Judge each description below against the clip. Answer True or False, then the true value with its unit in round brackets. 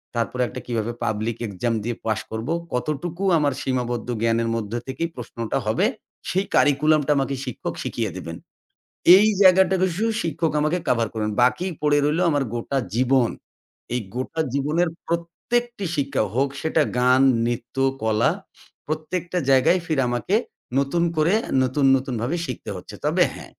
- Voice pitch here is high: False (135 Hz)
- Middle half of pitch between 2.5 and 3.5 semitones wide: False (5.4 semitones)